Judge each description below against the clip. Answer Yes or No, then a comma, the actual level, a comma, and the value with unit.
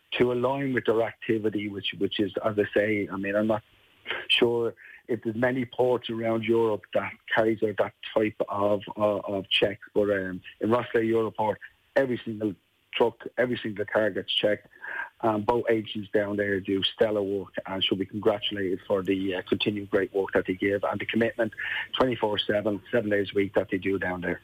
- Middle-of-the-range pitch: No, low, 105 Hz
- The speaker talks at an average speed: Yes, average, 195 wpm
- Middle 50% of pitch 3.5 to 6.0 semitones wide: No, narrow, 2.4 semitones